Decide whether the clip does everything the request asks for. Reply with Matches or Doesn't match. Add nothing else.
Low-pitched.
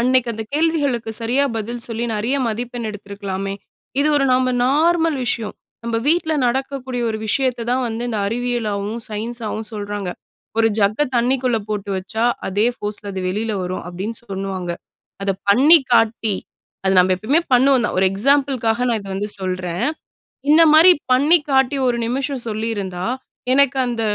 Doesn't match